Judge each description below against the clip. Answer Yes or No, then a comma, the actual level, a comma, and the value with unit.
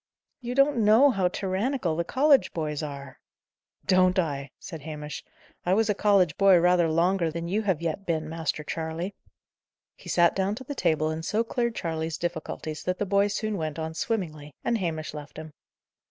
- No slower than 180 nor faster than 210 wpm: Yes, average, 185 wpm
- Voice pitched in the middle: Yes, medium, 175 Hz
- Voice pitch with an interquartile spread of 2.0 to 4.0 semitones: No, average, 4.4 semitones